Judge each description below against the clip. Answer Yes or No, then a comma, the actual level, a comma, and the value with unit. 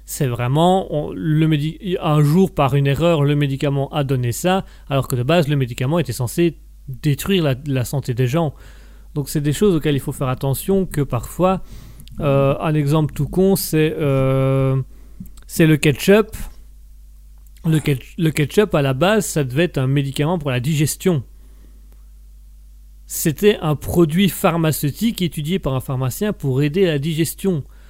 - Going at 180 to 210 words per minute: No, average, 170 wpm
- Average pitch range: Yes, average, 4.3 semitones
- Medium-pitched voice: Yes, medium, 145 Hz